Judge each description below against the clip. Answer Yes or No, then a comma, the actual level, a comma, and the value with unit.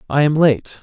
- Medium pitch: Yes, medium, 145 Hz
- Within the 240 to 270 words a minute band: No, fast, 215 wpm